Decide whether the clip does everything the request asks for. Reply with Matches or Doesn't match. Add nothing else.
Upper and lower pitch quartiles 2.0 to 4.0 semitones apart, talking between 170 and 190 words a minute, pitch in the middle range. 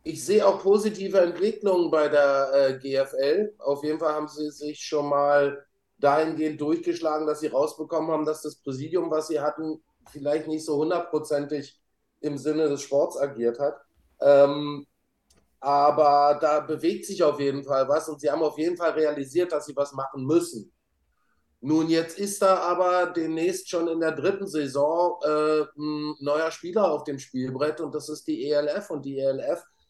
Matches